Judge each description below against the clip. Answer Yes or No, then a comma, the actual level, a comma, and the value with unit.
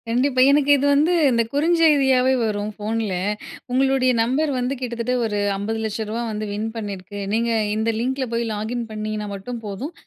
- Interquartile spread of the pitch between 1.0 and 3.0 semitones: No, average, 3.7 semitones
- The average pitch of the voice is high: Yes, high, 235 Hz